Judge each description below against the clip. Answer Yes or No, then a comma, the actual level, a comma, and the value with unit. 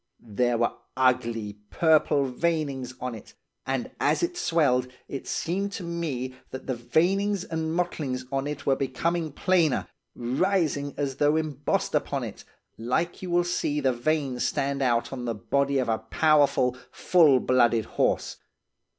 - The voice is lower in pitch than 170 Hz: Yes, medium, 140 Hz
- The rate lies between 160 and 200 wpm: No, average, 150 wpm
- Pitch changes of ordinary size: Yes, average, 4.3 semitones